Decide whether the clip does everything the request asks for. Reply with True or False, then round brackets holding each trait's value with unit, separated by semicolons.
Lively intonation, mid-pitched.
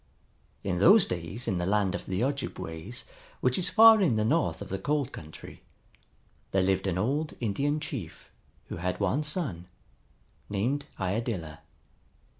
False (7.7 semitones; 105 Hz)